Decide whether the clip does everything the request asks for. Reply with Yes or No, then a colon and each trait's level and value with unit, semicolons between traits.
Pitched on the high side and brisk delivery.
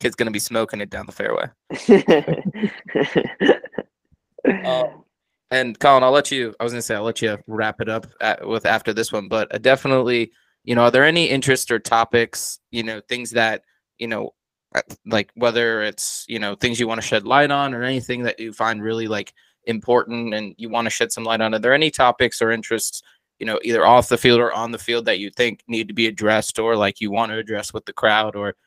No: low, 115 Hz; fast, 230 wpm